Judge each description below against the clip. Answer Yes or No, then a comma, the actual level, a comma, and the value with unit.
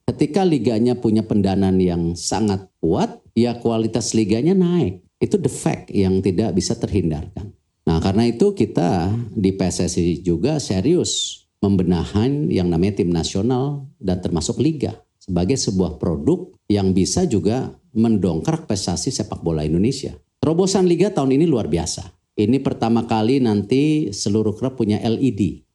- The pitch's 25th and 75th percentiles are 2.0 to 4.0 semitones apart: No, wide, 5.4 semitones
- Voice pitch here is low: Yes, low, 110 Hz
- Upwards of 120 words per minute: Yes, average, 135 wpm